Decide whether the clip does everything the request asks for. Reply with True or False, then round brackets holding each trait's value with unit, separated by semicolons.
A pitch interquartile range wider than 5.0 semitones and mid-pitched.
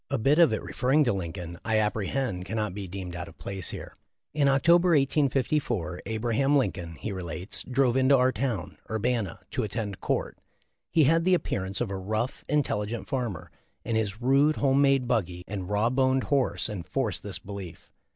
False (5.6 semitones; 115 Hz)